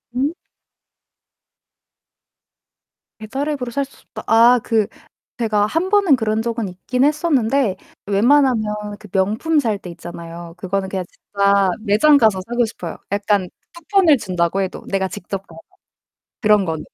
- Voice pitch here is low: No, high, 215 Hz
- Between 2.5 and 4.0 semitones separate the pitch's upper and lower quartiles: No, average, 5.3 semitones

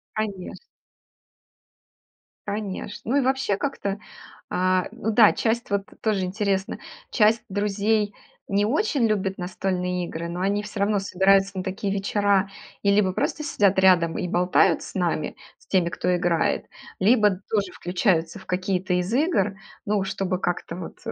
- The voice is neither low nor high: No, high, 195 Hz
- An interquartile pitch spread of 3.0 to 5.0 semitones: No, narrow, 2.4 semitones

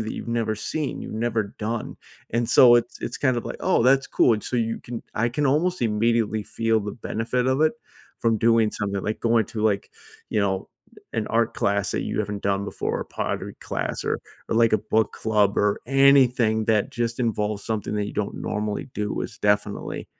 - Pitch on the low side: Yes, low, 110 Hz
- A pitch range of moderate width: No, narrow, 2.1 semitones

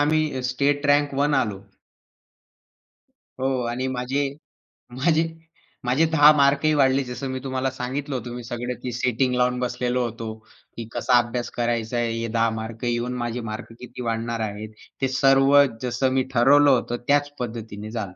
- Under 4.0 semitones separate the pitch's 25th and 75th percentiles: Yes, narrow, 2.5 semitones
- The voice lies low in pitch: Yes, low, 125 Hz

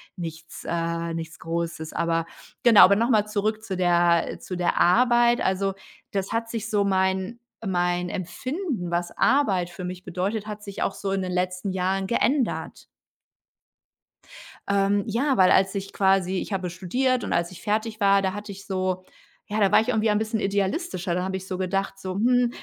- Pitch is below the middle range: No, high, 195 Hz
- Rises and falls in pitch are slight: No, average, 3.0 semitones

